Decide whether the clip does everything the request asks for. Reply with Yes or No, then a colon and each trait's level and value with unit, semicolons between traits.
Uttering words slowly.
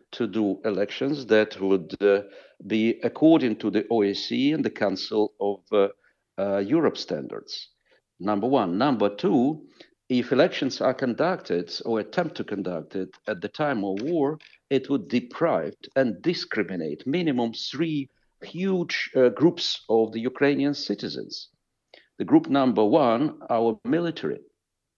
Yes: slow, 135 wpm